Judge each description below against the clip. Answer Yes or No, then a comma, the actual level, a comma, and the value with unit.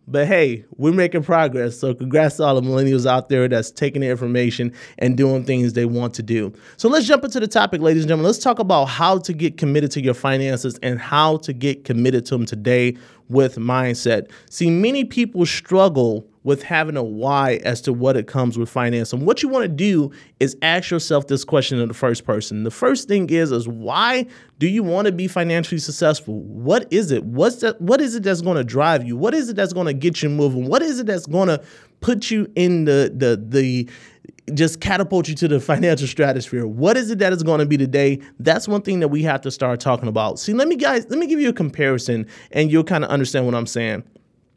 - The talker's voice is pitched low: No, medium, 145 Hz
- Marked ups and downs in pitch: Yes, wide, 6.0 semitones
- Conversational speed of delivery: No, fast, 230 wpm